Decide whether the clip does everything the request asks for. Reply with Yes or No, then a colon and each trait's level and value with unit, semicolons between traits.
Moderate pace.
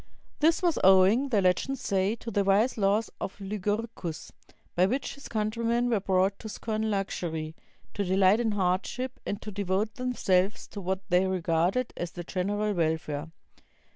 Yes: average, 160 wpm